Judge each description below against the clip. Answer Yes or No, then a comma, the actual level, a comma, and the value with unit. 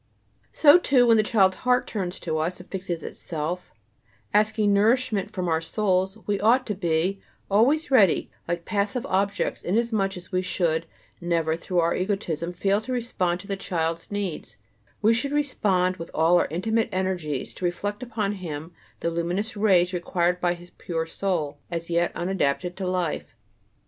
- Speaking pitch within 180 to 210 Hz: Yes, medium, 185 Hz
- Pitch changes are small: No, average, 3.5 semitones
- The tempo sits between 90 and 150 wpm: No, average, 165 wpm